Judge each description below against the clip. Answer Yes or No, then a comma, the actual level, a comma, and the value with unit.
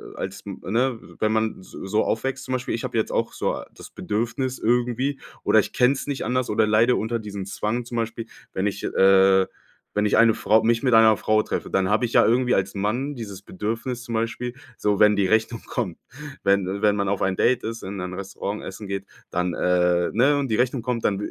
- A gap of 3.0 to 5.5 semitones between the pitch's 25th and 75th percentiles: Yes, average, 3.5 semitones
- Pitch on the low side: Yes, low, 110 Hz